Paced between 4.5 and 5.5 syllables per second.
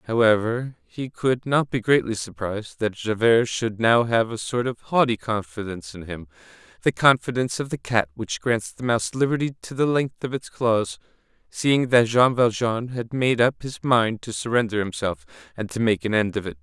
Yes: 5.0 syllables/s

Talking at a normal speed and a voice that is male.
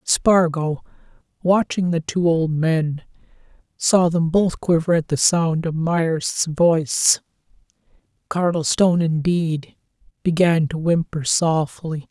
No: slow, 110 wpm; male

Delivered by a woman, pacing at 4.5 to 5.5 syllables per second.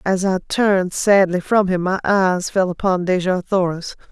Yes: female; 4.7 syllables/s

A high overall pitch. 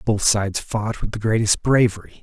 No: low, 110 Hz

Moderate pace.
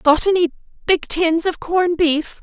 Yes: average, 175 wpm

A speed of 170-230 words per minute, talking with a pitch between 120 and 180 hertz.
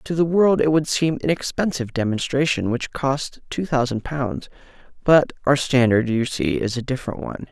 Yes: average, 185 wpm; low, 135 Hz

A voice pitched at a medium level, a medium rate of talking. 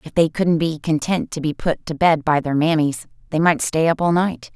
No: medium, 160 Hz; fast, 250 wpm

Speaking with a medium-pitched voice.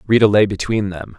No: low, 100 Hz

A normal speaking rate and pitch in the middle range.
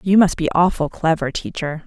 Yes: average, 195 wpm; medium, 165 Hz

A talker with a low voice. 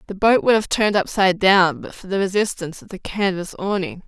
No: high, 195 Hz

